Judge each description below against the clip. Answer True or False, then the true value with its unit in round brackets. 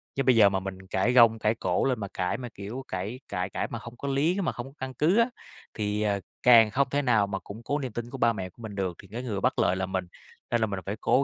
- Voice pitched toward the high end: False (115 Hz)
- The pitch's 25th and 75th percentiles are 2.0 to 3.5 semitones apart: False (4.4 semitones)